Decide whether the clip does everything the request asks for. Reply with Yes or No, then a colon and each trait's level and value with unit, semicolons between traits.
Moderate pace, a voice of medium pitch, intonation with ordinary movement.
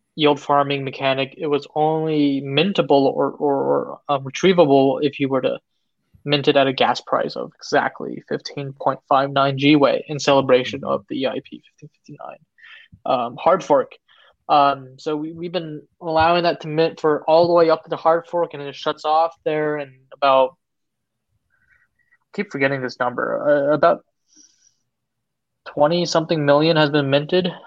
Yes: average, 170 wpm; medium, 150 Hz; average, 3.3 semitones